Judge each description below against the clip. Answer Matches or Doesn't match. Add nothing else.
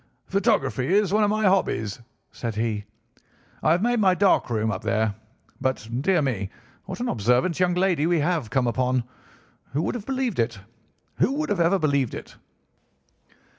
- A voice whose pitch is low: Doesn't match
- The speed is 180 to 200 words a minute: Doesn't match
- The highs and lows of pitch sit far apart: Matches